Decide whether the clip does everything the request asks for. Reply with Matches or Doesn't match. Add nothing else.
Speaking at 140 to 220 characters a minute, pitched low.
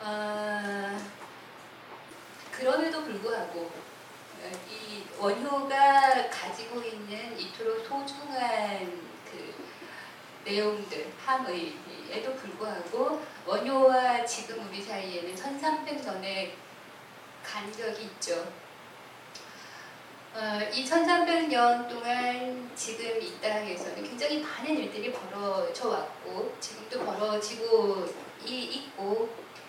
Doesn't match